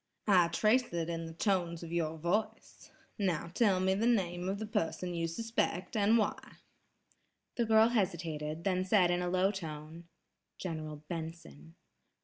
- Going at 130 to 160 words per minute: Yes, average, 155 wpm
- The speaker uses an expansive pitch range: No, average, 3.6 semitones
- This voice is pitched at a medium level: Yes, medium, 175 Hz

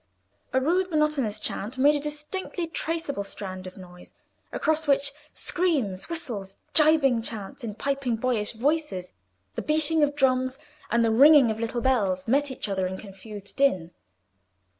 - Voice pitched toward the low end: No, very high, 260 Hz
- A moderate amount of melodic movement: No, wide, 6.3 semitones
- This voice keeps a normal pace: Yes, average, 150 wpm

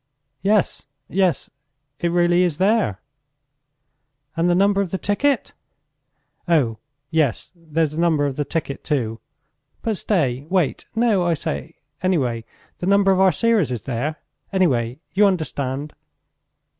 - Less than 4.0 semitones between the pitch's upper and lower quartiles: No, wide, 5.6 semitones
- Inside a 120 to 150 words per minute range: Yes, slow, 135 wpm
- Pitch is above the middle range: No, medium, 170 Hz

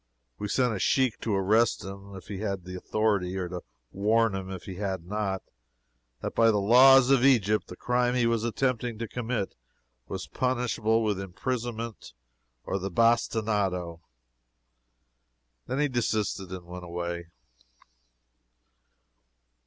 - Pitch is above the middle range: No, low, 105 Hz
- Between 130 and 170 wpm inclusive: Yes, average, 140 wpm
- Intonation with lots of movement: No, average, 3.7 semitones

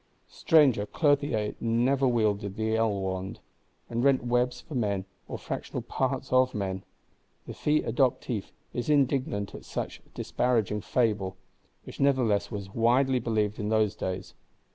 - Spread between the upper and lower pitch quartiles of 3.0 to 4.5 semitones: Yes, average, 4.0 semitones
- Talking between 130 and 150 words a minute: Yes, slow, 135 wpm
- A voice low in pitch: Yes, low, 115 Hz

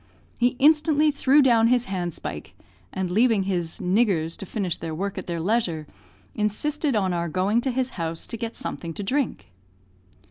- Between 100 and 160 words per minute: No, average, 170 wpm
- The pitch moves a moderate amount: No, wide, 6.0 semitones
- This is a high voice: Yes, high, 210 Hz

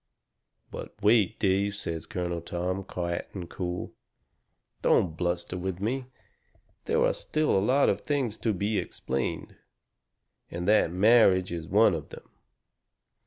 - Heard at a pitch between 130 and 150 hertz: No, very low, 95 Hz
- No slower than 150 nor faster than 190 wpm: No, slow, 135 wpm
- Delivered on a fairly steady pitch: No, average, 3.6 semitones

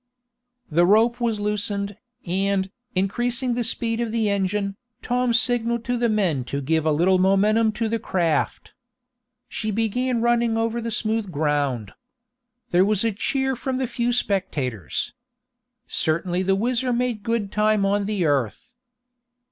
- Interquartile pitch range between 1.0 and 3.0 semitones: No, average, 4.0 semitones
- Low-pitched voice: No, high, 210 Hz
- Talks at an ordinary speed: Yes, average, 150 wpm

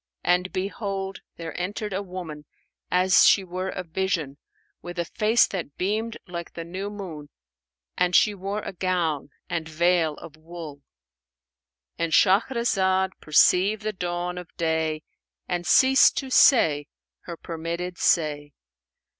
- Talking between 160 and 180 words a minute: No, slow, 135 wpm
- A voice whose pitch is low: No, medium, 180 Hz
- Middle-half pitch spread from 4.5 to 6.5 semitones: No, average, 2.8 semitones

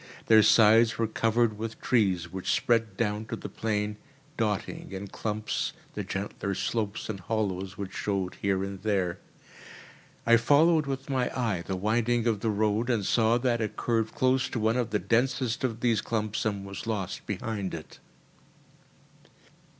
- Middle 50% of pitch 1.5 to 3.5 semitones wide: Yes, average, 2.8 semitones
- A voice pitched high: No, low, 110 Hz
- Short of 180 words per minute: Yes, average, 165 wpm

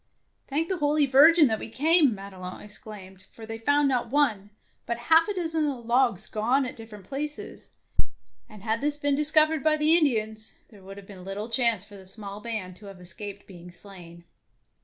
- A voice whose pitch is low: No, high, 225 Hz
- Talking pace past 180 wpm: Yes, average, 200 wpm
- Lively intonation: Yes, wide, 6.5 semitones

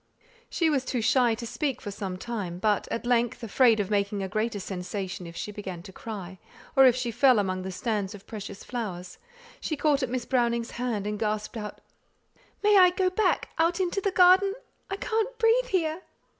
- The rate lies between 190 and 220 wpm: Yes, average, 200 wpm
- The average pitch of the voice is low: No, high, 235 Hz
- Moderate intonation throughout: No, wide, 7.1 semitones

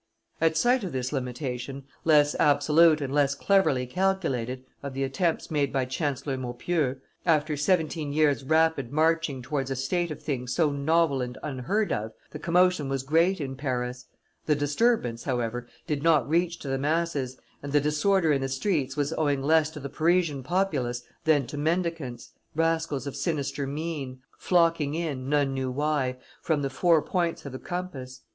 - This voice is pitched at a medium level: Yes, medium, 145 Hz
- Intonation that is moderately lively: Yes, average, 3.6 semitones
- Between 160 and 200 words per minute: Yes, average, 170 wpm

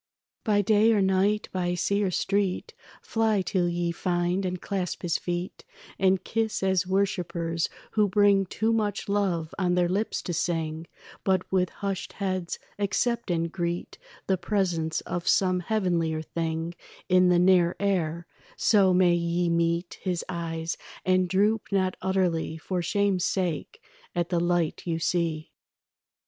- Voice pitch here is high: No, medium, 180 Hz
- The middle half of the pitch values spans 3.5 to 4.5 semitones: No, narrow, 2.4 semitones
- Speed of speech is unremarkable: Yes, average, 150 wpm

